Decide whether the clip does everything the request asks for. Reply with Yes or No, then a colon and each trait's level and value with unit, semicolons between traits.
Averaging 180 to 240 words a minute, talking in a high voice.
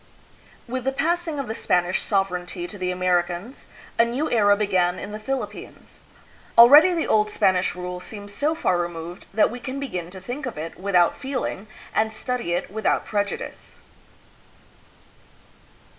No: average, 155 wpm; high, 205 Hz